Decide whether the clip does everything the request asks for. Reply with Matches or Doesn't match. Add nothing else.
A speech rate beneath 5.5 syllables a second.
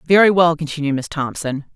Doesn't match